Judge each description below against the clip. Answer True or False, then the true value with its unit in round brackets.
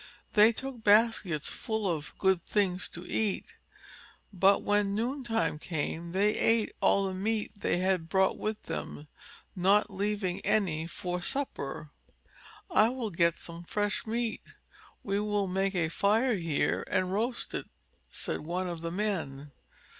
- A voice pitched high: True (195 Hz)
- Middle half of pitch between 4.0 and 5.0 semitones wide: False (3.6 semitones)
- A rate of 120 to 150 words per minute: True (145 wpm)